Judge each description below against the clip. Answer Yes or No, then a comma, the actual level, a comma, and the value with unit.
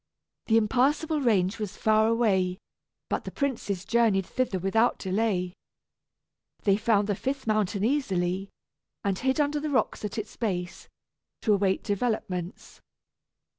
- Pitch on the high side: Yes, high, 215 Hz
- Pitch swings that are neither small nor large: Yes, average, 4.0 semitones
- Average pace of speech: No, slow, 130 wpm